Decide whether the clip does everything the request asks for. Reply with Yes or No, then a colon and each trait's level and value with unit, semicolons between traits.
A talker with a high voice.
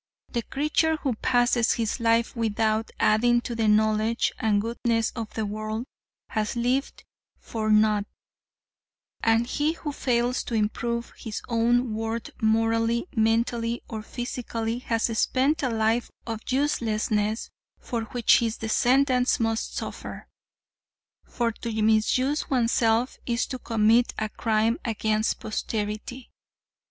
Yes: high, 230 Hz